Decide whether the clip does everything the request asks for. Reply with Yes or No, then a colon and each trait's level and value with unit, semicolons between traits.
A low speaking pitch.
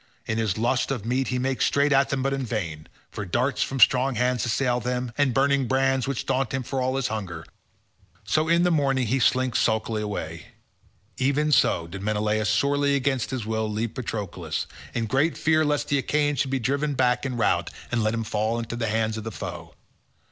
Yes: low, 125 Hz